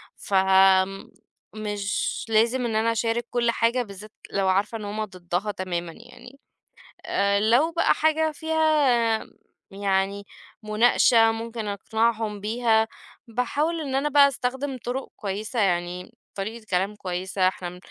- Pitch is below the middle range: No, high, 215 Hz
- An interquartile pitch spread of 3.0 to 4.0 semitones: Yes, average, 3.7 semitones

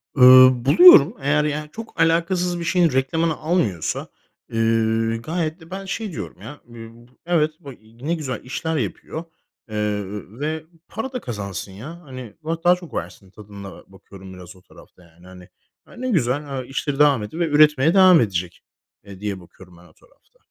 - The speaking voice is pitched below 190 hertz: Yes, low, 135 Hz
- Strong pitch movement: Yes, wide, 7.7 semitones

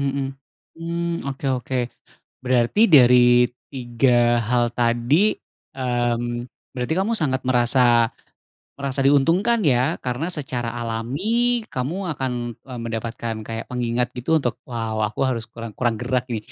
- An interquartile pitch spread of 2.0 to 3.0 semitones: Yes, narrow, 2.5 semitones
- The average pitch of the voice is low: Yes, low, 125 Hz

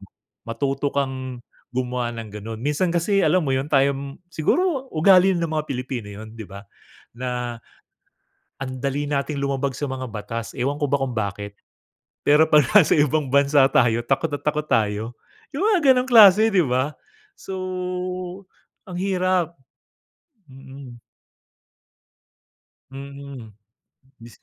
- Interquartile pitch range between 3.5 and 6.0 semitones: Yes, average, 4.2 semitones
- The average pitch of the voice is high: No, medium, 140 Hz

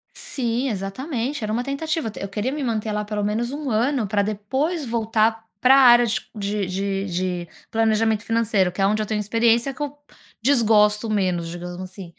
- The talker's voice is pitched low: No, high, 220 Hz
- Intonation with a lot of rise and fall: No, average, 3.3 semitones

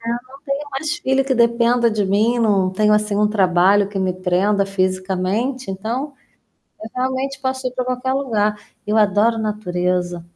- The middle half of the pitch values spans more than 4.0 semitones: Yes, average, 4.7 semitones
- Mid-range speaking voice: No, high, 215 Hz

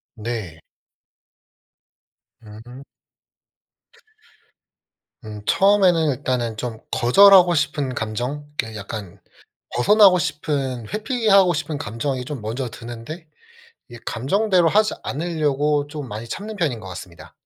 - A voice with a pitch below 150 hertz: Yes, medium, 140 Hz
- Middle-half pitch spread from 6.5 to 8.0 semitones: Yes, wide, 6.9 semitones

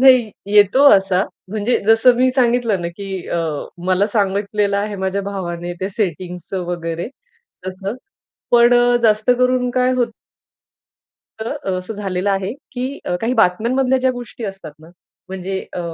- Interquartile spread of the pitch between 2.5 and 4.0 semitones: No, average, 4.4 semitones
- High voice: Yes, high, 205 Hz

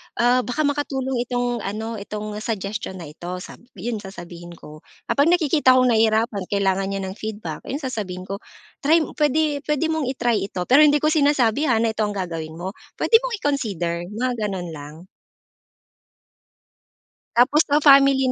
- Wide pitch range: Yes, wide, 6.4 semitones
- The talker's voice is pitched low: No, high, 230 Hz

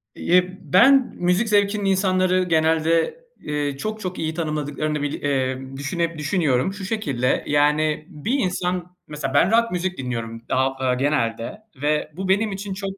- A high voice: No, medium, 160 Hz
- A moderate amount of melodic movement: Yes, average, 4.8 semitones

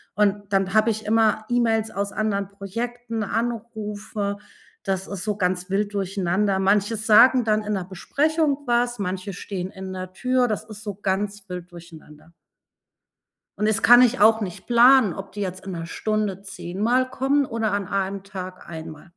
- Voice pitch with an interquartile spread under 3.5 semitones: Yes, average, 2.9 semitones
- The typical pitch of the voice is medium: No, high, 205 Hz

